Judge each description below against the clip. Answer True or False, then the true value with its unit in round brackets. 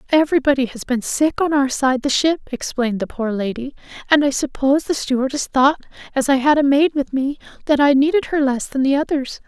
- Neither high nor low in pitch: False (275 Hz)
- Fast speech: True (215 wpm)